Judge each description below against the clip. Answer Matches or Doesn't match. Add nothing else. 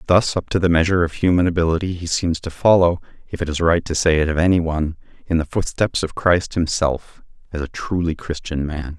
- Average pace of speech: Doesn't match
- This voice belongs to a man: Matches